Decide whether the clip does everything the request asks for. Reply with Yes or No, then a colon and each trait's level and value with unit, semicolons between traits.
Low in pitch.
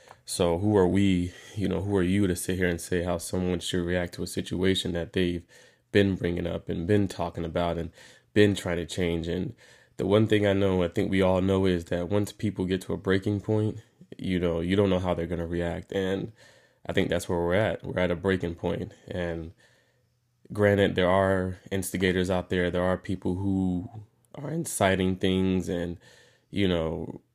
Yes: very low, 95 Hz